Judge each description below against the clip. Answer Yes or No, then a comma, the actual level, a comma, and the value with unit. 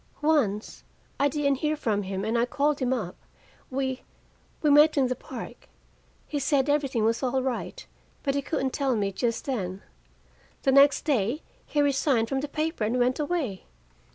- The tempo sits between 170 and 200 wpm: Yes, average, 175 wpm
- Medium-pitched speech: No, very high, 265 Hz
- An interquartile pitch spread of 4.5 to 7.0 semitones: No, average, 3.9 semitones